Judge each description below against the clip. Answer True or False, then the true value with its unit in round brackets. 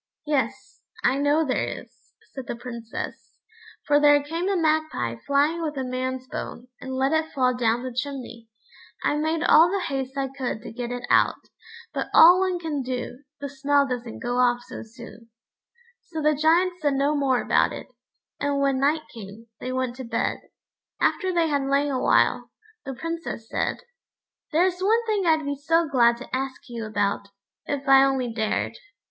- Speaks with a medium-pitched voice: False (275 Hz)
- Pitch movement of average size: True (3.9 semitones)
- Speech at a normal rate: True (185 wpm)